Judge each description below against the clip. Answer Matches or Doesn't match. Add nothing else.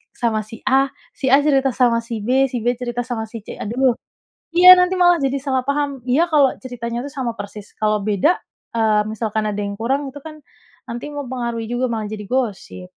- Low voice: Doesn't match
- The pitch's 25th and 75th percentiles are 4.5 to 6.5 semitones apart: Doesn't match